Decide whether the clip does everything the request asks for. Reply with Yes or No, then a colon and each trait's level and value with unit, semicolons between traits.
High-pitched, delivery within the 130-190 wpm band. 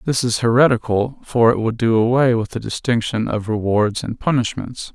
No: low, 115 Hz; average, 180 wpm